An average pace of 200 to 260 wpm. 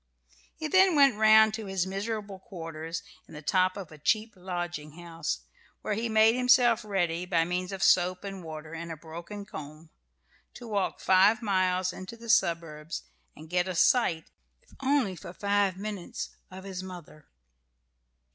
No: average, 165 wpm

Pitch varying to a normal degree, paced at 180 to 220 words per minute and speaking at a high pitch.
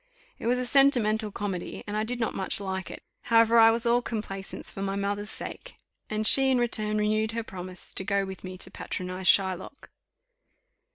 Yes: average, 3.0 semitones; average, 190 wpm; high, 215 Hz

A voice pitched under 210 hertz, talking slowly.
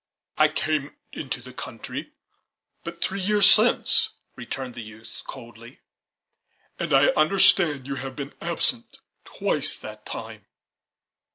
Yes: medium, 140 Hz; slow, 120 wpm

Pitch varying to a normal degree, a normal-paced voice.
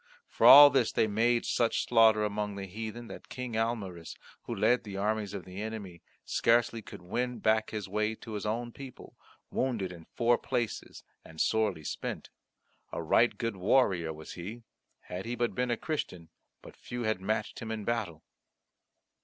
Yes: average, 3.4 semitones; average, 175 wpm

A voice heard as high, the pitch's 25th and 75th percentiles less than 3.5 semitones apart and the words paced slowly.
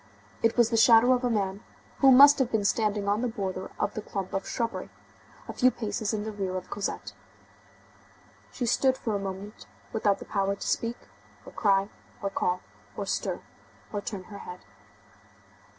No: high, 210 Hz; average, 2.8 semitones; average, 180 wpm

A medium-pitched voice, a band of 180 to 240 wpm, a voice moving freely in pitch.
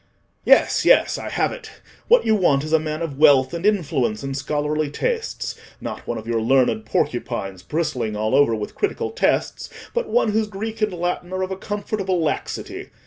Yes: medium, 155 Hz; average, 185 wpm; wide, 7.6 semitones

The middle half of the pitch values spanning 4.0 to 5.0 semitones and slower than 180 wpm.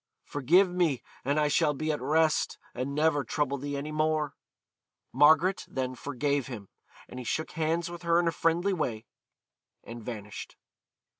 No: average, 3.4 semitones; average, 160 wpm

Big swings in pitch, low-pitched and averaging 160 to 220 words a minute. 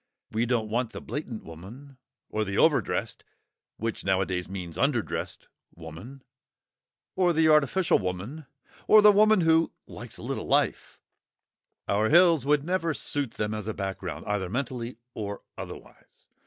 No: wide, 7.6 semitones; low, 120 Hz; average, 140 wpm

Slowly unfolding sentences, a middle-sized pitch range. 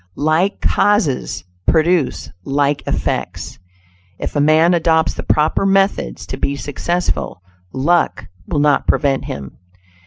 Yes: slow, 120 wpm; average, 3.7 semitones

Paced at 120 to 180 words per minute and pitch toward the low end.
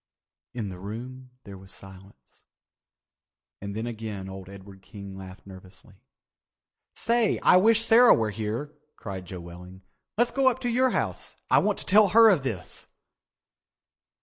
Yes: average, 150 wpm; low, 105 Hz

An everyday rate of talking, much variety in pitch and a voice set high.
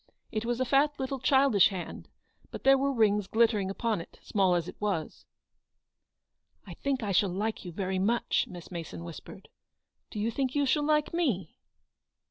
Yes: average, 180 wpm; wide, 6.0 semitones; high, 220 Hz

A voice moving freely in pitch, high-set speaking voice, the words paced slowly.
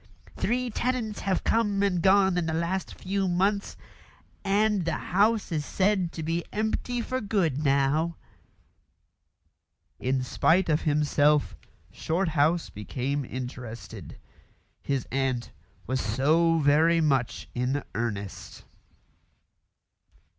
No: wide, 6.0 semitones; medium, 165 Hz; slow, 110 wpm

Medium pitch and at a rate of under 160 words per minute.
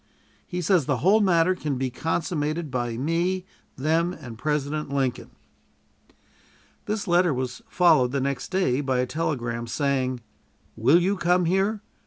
Yes: medium, 150 Hz; average, 145 wpm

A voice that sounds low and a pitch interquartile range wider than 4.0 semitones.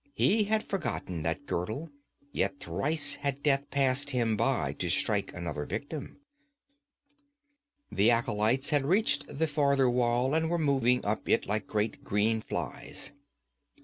Yes: low, 130 Hz; average, 5.2 semitones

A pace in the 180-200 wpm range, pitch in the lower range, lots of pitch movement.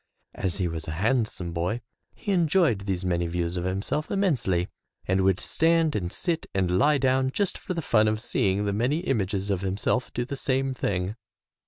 Yes: average, 190 wpm; low, 105 Hz; wide, 6.7 semitones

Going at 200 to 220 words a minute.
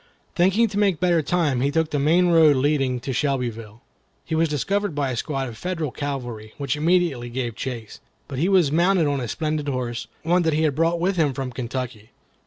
Yes: fast, 205 wpm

